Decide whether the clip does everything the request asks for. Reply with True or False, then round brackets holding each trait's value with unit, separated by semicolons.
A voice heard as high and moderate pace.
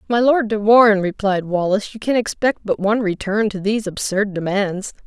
True (205 Hz; 190 wpm)